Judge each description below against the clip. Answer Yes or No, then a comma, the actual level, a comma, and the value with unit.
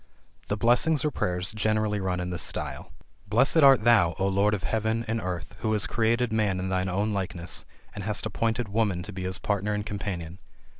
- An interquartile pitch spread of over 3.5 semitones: No, average, 3.2 semitones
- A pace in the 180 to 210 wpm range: Yes, average, 200 wpm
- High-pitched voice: No, low, 105 Hz